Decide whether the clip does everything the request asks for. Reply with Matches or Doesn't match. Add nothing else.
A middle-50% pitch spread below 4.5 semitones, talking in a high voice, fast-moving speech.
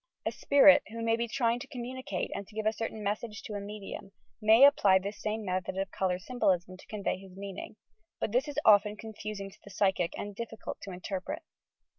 Matches